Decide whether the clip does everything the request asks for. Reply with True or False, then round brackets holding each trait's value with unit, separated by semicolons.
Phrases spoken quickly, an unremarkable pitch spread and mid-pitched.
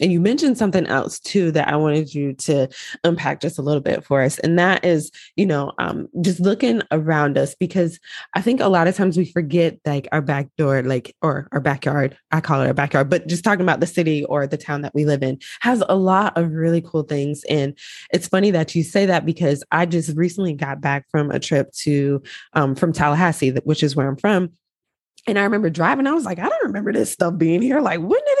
True (235 wpm; 3.9 semitones; 165 Hz)